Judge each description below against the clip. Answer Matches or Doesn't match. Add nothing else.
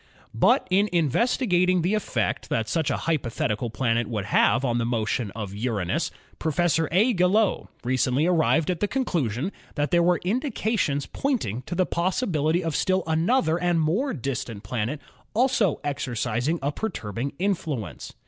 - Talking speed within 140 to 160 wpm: Matches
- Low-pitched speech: Doesn't match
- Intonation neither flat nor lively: Doesn't match